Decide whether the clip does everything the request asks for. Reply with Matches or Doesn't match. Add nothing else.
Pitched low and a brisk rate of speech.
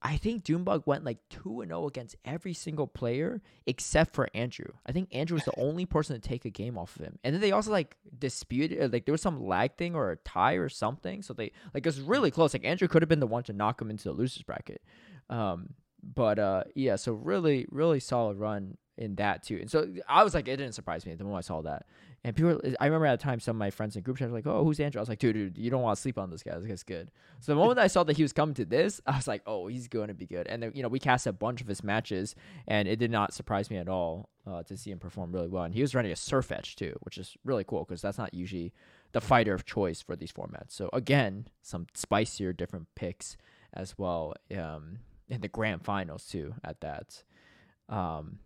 Matches